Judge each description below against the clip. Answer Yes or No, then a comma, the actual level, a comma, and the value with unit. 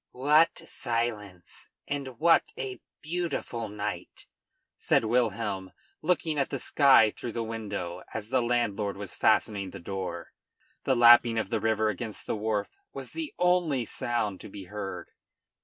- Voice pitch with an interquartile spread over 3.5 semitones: Yes, average, 4.2 semitones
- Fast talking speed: No, average, 145 wpm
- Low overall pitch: Yes, low, 115 Hz